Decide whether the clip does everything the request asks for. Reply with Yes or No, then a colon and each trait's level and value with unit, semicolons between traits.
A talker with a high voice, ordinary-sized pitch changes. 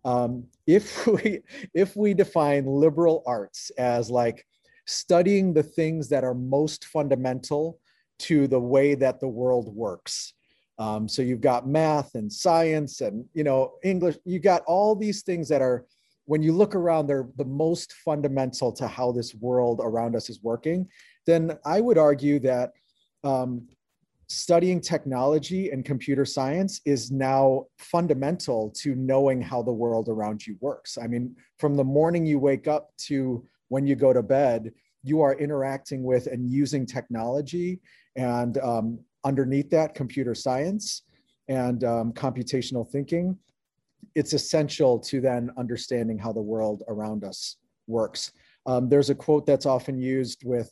No: low, 135 Hz; average, 3.9 semitones